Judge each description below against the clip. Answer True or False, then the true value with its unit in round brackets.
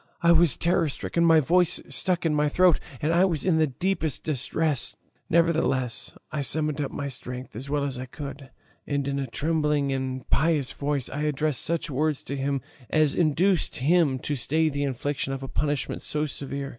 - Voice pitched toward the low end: False (150 Hz)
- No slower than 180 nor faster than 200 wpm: True (190 wpm)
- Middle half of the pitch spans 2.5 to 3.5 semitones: True (2.8 semitones)